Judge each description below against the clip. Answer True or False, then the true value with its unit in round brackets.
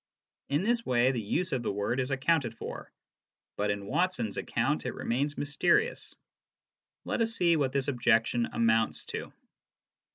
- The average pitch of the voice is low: True (130 Hz)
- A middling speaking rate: True (155 wpm)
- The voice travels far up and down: True (5.8 semitones)